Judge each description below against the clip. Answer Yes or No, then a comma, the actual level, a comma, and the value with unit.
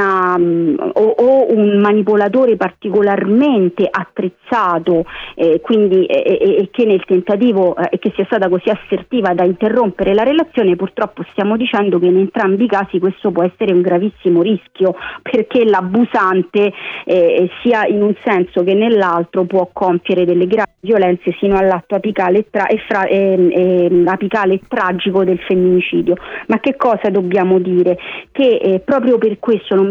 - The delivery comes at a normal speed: Yes, average, 150 wpm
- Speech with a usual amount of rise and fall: Yes, average, 3.0 semitones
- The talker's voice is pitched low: No, high, 195 Hz